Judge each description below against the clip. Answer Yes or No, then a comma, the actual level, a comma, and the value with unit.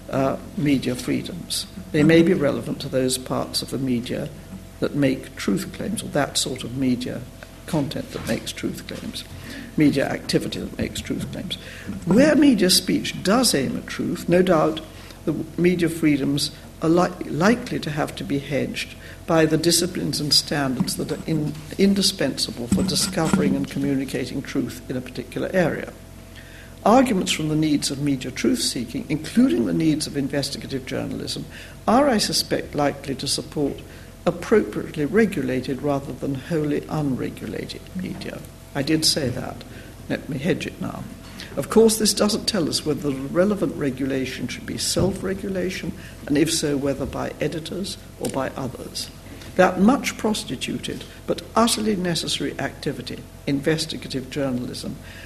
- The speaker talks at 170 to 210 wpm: No, average, 150 wpm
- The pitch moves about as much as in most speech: Yes, average, 4.9 semitones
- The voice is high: No, medium, 150 Hz